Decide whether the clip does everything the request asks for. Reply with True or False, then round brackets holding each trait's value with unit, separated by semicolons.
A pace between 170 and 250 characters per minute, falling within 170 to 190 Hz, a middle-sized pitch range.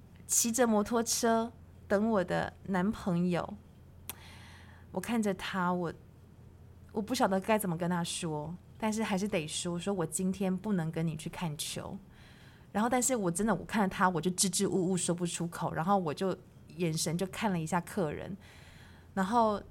True (240 characters per minute; 185 Hz; 3.5 semitones)